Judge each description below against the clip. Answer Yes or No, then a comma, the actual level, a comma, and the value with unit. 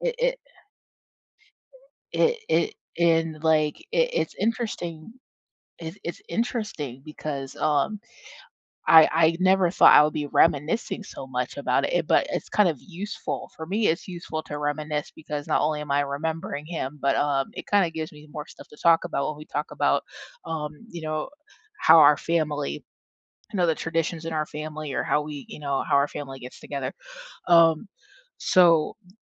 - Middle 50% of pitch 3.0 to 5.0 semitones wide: No, narrow, 2.4 semitones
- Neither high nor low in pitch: Yes, medium, 155 Hz